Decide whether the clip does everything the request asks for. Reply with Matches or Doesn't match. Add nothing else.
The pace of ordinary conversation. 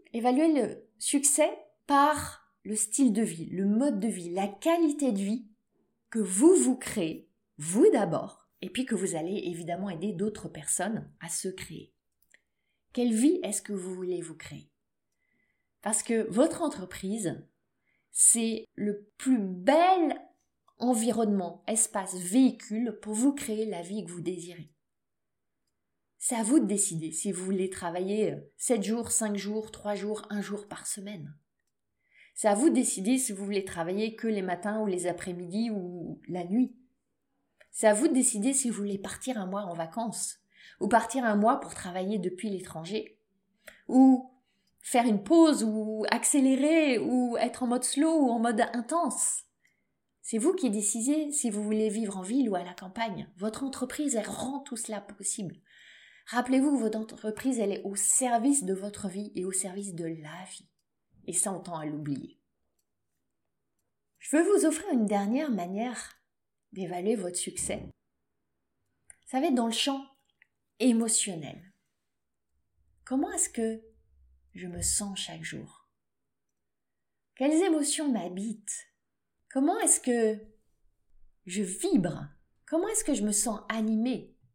Matches